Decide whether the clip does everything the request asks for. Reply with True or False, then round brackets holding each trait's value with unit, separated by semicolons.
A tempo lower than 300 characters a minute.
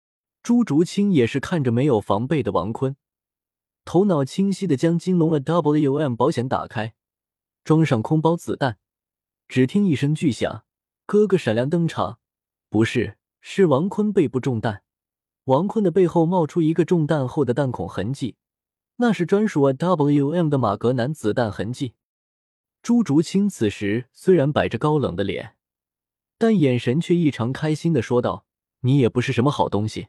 True (240 characters per minute)